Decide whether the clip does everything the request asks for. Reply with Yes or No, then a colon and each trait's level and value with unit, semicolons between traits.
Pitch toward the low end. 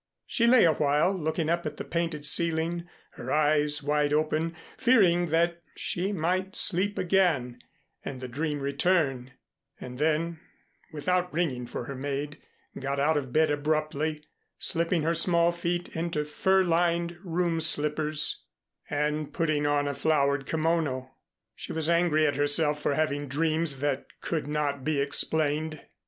No: medium, 155 Hz